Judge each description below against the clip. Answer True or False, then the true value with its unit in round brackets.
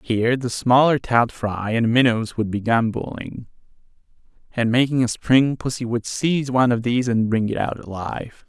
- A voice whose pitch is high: False (120 Hz)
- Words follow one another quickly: False (175 wpm)